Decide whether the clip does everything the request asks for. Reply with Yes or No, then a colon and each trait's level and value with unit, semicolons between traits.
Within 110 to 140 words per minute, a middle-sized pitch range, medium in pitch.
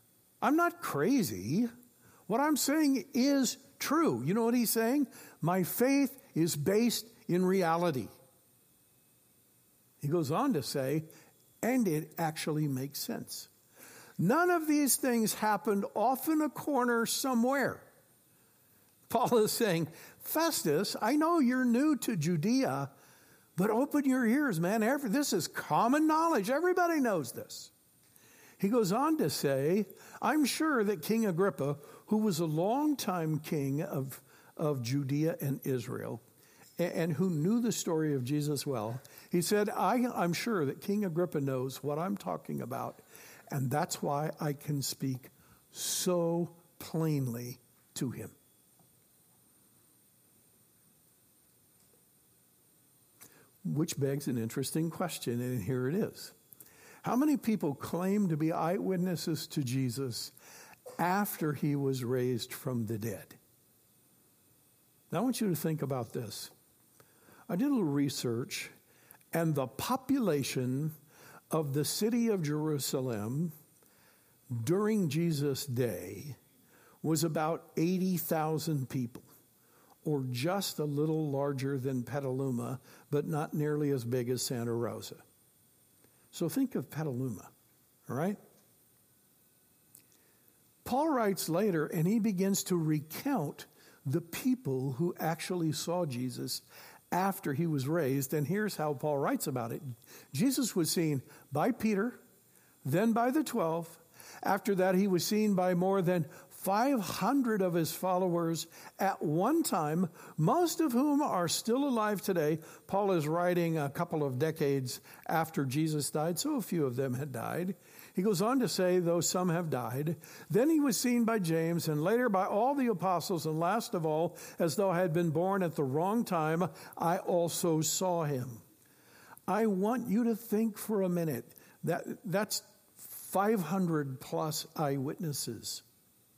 No: slow, 135 wpm; wide, 6.5 semitones; medium, 170 Hz